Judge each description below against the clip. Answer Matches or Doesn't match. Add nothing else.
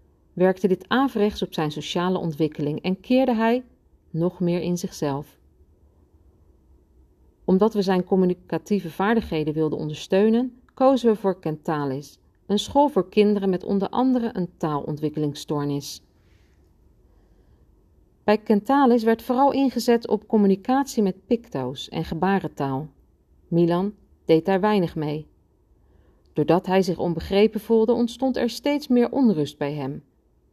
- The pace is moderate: Doesn't match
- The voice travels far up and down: Matches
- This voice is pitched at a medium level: Matches